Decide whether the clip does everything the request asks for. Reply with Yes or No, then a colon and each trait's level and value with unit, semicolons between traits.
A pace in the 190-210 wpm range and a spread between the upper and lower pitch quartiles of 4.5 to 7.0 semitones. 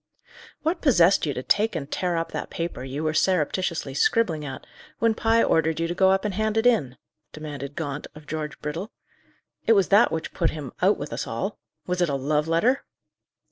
Yes: fast, 205 wpm; average, 5.0 semitones